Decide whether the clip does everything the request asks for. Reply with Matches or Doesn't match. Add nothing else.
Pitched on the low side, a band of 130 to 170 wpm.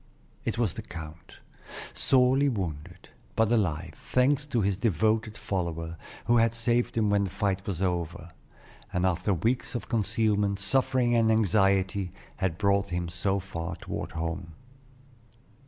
Matches